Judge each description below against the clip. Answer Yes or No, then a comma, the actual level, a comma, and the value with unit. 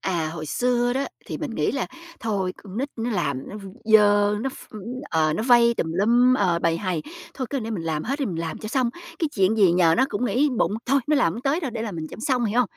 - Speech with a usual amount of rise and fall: No, wide, 6.1 semitones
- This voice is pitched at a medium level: No, high, 220 Hz